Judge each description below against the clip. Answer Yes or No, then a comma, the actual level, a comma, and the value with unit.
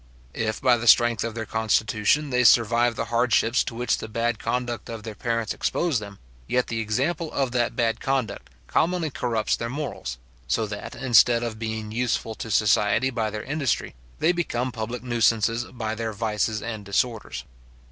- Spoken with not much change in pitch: Yes, narrow, 2.1 semitones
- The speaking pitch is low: Yes, low, 115 Hz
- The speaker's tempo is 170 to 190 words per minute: Yes, average, 175 wpm